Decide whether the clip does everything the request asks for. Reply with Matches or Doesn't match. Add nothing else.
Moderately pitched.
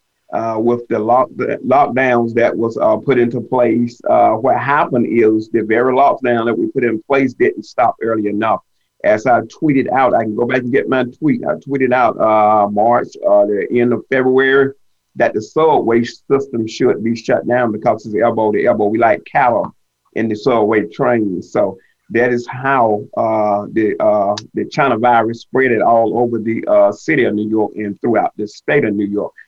Doesn't match